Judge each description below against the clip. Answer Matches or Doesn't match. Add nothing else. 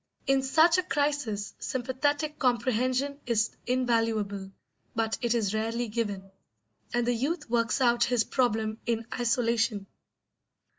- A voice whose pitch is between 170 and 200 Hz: Doesn't match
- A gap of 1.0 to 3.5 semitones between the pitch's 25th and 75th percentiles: Matches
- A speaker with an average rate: Doesn't match